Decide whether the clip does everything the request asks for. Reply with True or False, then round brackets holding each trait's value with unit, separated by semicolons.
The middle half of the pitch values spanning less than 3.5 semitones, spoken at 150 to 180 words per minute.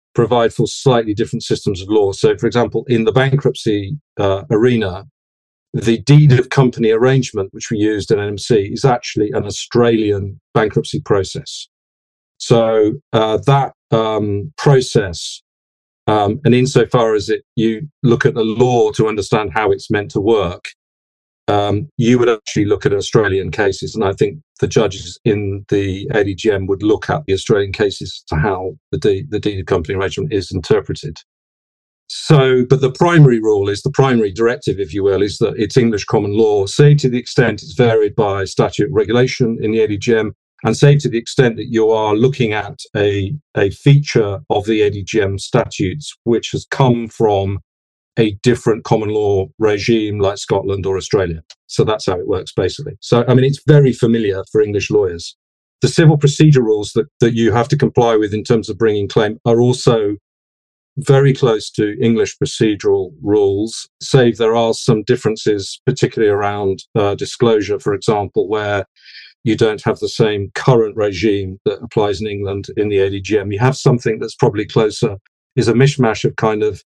False (4.2 semitones; 175 wpm)